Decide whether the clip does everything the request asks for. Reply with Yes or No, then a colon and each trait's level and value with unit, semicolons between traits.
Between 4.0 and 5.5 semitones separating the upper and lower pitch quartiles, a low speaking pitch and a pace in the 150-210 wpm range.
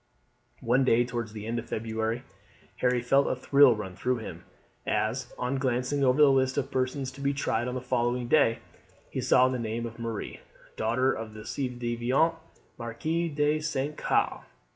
No: narrow, 2.5 semitones; low, 125 Hz; average, 180 wpm